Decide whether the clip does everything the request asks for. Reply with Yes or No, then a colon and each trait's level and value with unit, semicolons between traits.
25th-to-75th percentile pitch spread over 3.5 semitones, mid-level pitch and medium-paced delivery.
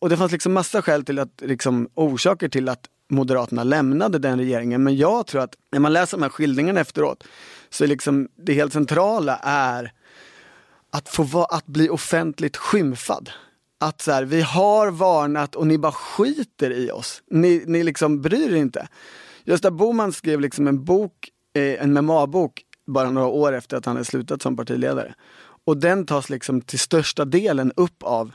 Yes: average, 4.4 semitones; medium, 150 Hz; average, 180 wpm